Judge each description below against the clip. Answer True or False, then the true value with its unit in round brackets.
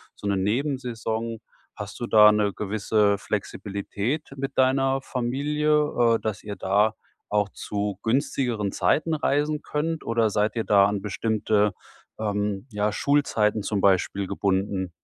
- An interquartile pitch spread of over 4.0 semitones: True (4.4 semitones)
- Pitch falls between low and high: False (110 Hz)